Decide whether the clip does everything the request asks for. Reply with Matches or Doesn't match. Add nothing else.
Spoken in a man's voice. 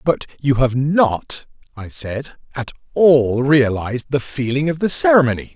Matches